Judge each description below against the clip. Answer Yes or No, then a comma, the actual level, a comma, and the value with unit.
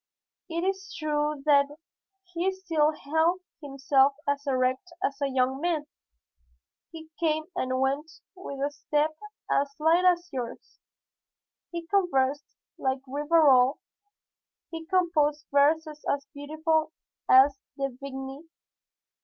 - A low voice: No, very high, 295 Hz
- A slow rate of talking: Yes, slow, 115 wpm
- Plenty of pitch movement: No, average, 3.1 semitones